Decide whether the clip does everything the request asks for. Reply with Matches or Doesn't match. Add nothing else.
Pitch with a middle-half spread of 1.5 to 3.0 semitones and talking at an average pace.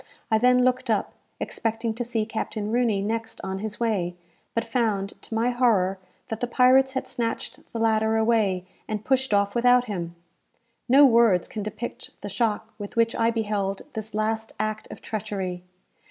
Matches